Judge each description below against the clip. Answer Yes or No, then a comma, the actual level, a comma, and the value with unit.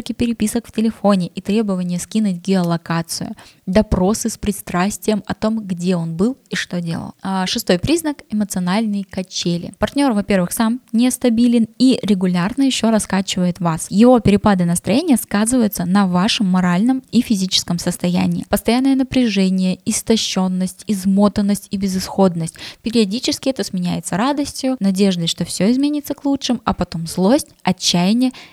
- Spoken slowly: No, average, 130 wpm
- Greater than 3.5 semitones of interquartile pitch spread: Yes, average, 4.0 semitones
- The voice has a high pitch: Yes, high, 205 Hz